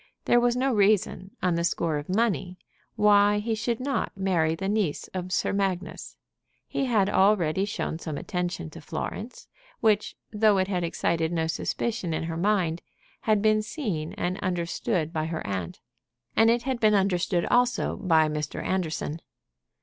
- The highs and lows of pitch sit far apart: No, average, 4.3 semitones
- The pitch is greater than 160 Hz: Yes, high, 190 Hz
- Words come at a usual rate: Yes, average, 165 wpm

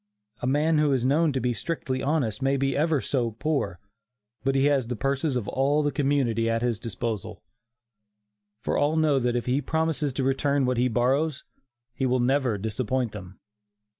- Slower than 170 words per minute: No, average, 185 wpm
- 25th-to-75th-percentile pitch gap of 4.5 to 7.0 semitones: No, average, 3.1 semitones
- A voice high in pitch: No, low, 130 Hz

